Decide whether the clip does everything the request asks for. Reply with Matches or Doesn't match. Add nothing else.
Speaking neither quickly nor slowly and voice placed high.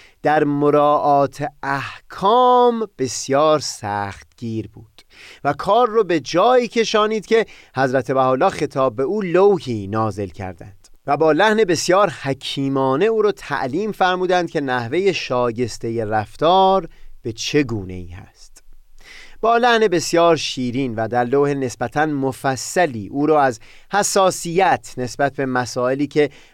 Doesn't match